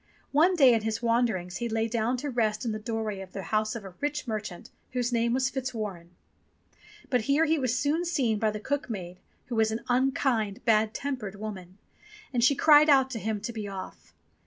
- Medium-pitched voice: No, high, 230 Hz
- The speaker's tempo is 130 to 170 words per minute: No, fast, 205 wpm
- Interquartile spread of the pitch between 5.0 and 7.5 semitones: No, average, 3.5 semitones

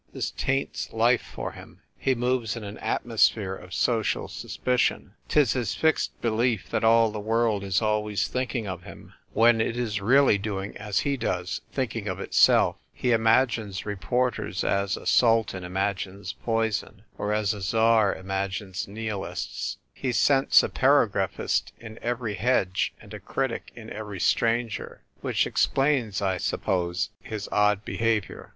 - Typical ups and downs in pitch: Yes, average, 3.0 semitones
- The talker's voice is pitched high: No, low, 110 Hz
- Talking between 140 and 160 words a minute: Yes, average, 155 wpm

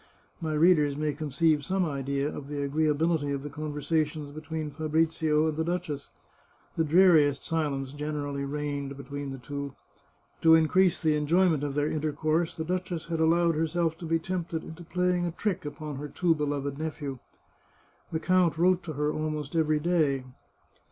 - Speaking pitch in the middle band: Yes, medium, 155 Hz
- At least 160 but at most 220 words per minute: Yes, average, 165 wpm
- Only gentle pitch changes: Yes, narrow, 2.3 semitones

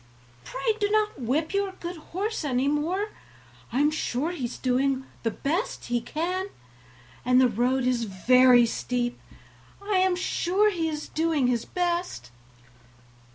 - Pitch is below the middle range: No, very high, 295 Hz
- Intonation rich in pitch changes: Yes, wide, 6.3 semitones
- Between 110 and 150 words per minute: Yes, average, 145 wpm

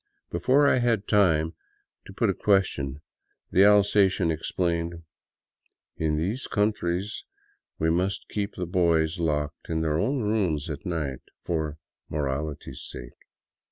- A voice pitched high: No, very low, 85 Hz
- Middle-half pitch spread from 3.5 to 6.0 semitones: Yes, average, 4.5 semitones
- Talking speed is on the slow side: Yes, slow, 130 wpm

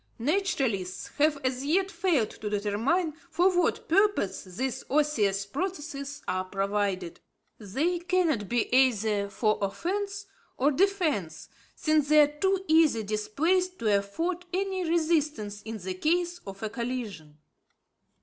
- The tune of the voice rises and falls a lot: Yes, wide, 9.0 semitones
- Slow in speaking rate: Yes, slow, 130 wpm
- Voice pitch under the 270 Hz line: No, very high, 280 Hz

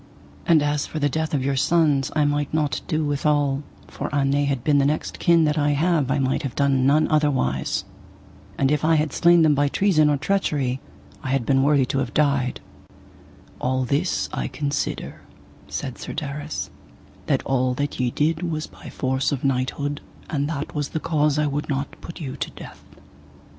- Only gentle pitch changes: Yes, narrow, 2.0 semitones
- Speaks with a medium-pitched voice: Yes, medium, 145 Hz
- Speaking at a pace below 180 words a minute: No, average, 195 wpm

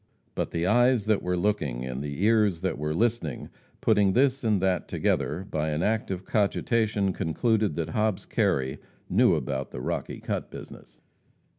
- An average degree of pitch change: No, wide, 6.1 semitones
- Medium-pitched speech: No, very low, 95 Hz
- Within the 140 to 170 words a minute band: Yes, average, 165 wpm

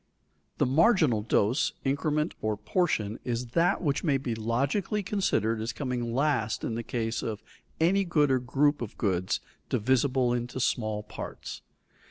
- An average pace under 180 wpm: Yes, average, 155 wpm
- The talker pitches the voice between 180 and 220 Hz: No, low, 125 Hz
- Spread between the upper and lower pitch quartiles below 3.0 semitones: No, average, 4.9 semitones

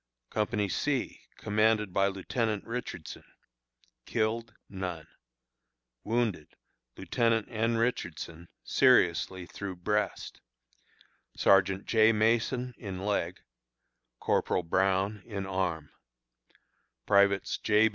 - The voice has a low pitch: Yes, low, 105 Hz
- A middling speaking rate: No, slow, 85 wpm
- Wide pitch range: No, average, 3.1 semitones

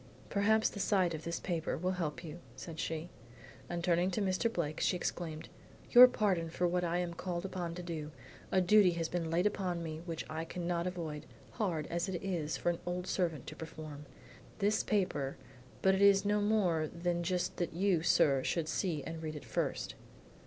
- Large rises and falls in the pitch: No, narrow, 2.5 semitones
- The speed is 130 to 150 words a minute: No, average, 195 wpm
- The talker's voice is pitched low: No, medium, 175 Hz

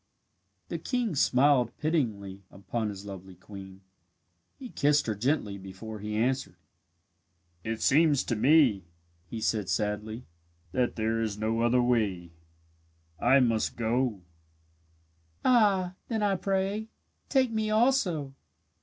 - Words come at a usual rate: No, slow, 120 wpm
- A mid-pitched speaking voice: No, low, 120 Hz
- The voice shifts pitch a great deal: Yes, wide, 7.2 semitones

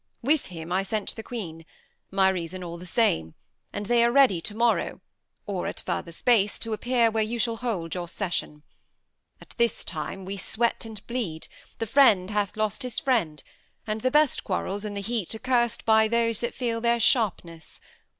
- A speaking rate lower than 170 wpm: No, average, 190 wpm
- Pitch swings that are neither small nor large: Yes, average, 4.2 semitones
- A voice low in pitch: No, high, 215 Hz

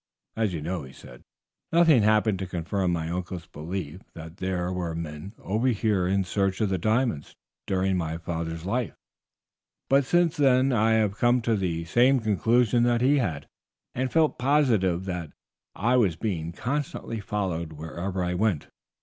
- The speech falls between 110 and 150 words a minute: No, average, 165 wpm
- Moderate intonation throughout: No, wide, 5.7 semitones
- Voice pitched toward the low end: Yes, very low, 95 Hz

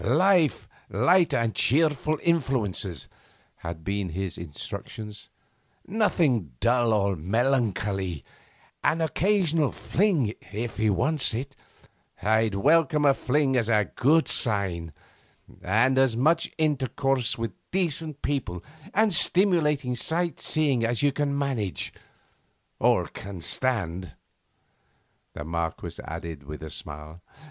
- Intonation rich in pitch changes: Yes, wide, 7.7 semitones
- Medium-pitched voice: No, low, 120 Hz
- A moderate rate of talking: No, slow, 115 wpm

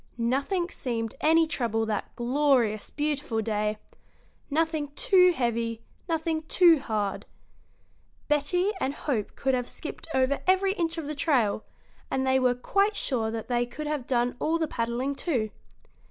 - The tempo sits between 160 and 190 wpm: No, average, 150 wpm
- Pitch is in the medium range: No, very high, 265 Hz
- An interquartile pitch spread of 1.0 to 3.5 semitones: No, wide, 5.4 semitones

